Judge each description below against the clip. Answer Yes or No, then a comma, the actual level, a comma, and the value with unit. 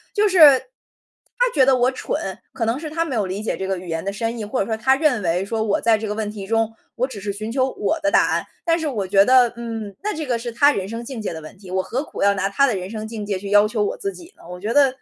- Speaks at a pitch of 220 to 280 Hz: Yes, high, 225 Hz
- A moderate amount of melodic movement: Yes, average, 4.8 semitones